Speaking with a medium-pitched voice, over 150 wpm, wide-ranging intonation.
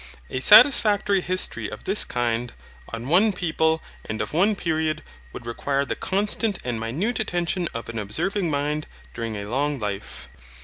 Yes: medium, 155 Hz; average, 160 wpm; wide, 8.5 semitones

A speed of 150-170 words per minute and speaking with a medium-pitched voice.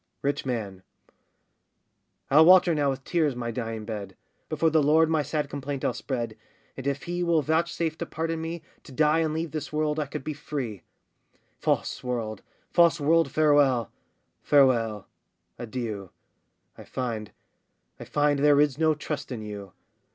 Yes: average, 160 wpm; medium, 145 Hz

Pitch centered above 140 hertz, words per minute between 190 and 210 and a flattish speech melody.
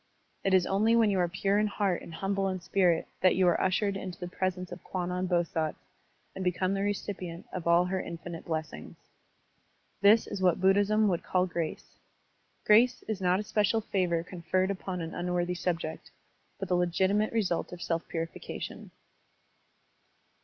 No: medium, 185 Hz; average, 165 wpm; narrow, 2.2 semitones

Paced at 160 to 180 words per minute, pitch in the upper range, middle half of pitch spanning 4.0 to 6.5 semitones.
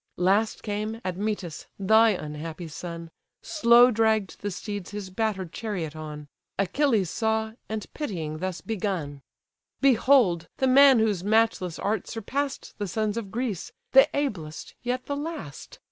No: slow, 135 wpm; high, 210 Hz; average, 4.4 semitones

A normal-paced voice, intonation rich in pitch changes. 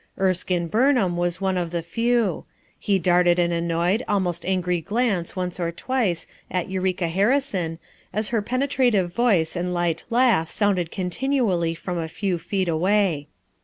No: average, 155 wpm; average, 3.5 semitones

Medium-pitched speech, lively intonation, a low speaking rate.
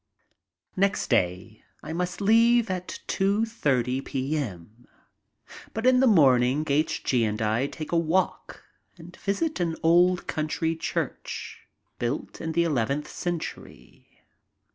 Yes: medium, 160 Hz; wide, 6.3 semitones; slow, 120 wpm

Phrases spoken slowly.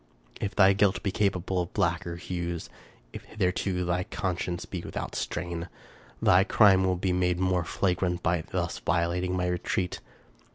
No: average, 160 wpm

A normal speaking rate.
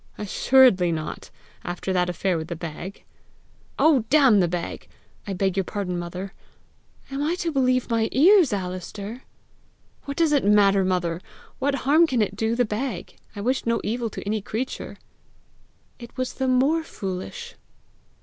Yes: average, 160 wpm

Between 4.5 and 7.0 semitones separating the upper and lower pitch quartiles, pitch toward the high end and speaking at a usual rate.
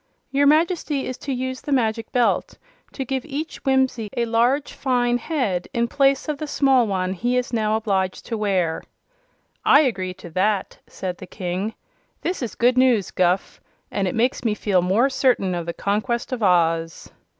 Yes: wide, 5.6 semitones; high, 235 Hz; average, 180 wpm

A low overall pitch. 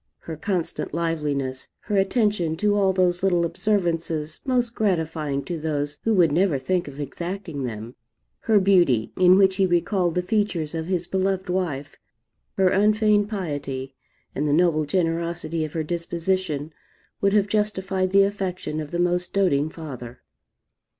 No: medium, 175 Hz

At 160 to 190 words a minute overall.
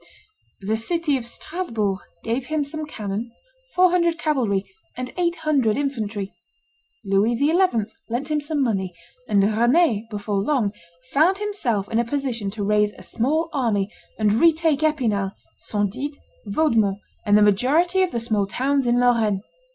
No: average, 150 wpm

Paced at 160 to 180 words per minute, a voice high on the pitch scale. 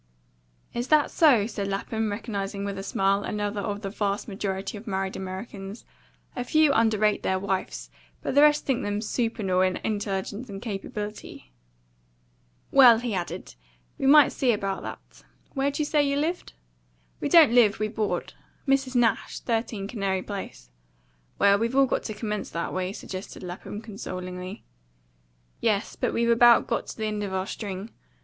Yes: average, 165 wpm; high, 210 Hz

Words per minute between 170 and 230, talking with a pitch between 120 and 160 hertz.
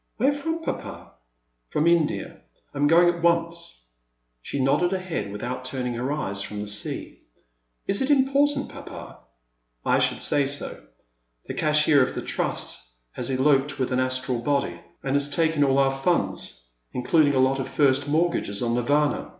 Yes: average, 175 wpm; medium, 140 Hz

